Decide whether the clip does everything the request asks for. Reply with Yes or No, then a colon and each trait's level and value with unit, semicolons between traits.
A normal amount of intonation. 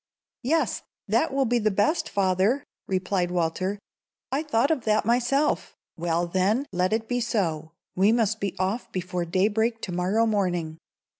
Yes: average, 4.5 semitones